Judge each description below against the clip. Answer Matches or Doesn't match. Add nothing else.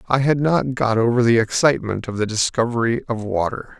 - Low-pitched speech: Matches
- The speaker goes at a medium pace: Matches